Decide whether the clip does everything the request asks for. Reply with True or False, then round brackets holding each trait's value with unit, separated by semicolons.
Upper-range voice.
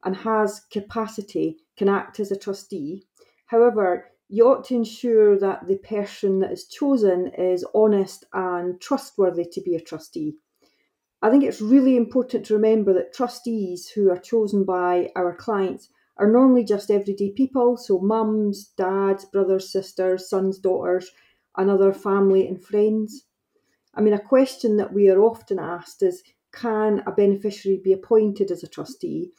True (205 Hz)